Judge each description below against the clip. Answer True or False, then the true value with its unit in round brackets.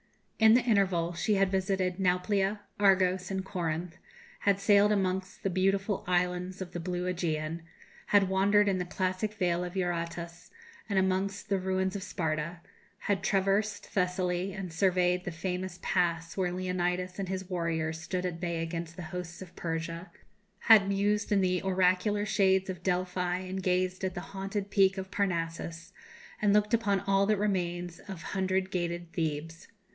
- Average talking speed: True (160 wpm)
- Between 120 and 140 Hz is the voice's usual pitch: False (185 Hz)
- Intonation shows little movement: True (1.8 semitones)